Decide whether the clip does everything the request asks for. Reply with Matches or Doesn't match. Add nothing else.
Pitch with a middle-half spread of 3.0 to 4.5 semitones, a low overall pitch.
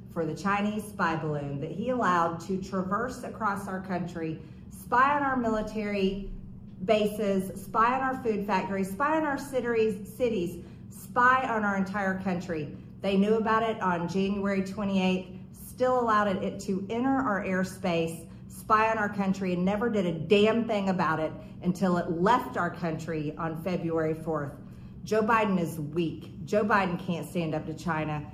Doesn't match